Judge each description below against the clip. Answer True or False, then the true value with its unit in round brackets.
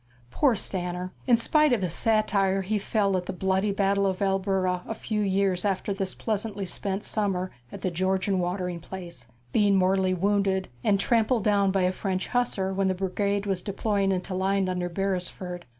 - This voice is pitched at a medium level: False (195 Hz)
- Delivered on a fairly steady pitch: True (1.6 semitones)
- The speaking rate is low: False (180 wpm)